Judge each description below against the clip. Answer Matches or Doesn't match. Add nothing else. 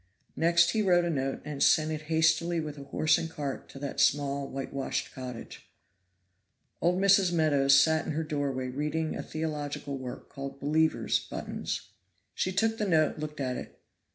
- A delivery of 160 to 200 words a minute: Matches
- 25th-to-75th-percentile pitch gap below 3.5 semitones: Matches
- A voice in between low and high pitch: Matches